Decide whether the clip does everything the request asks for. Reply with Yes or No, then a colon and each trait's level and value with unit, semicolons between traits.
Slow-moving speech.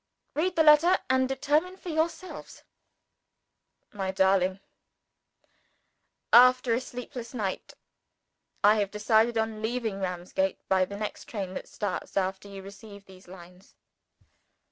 Yes: slow, 120 wpm